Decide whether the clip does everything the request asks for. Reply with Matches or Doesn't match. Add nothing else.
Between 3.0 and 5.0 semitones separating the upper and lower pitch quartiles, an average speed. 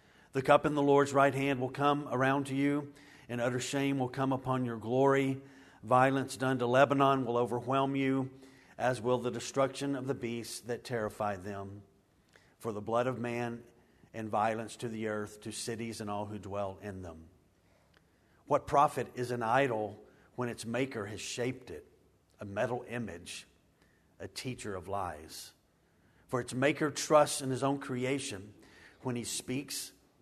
Matches